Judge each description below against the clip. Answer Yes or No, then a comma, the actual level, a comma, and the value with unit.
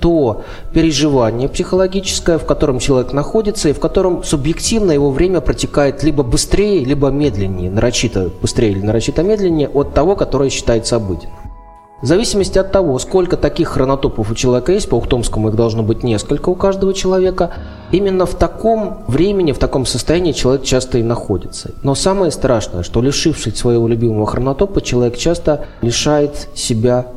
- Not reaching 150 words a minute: No, average, 155 wpm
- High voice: No, medium, 140 Hz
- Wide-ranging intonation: Yes, wide, 6.3 semitones